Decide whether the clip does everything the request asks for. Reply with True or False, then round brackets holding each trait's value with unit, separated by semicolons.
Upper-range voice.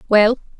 True (220 Hz)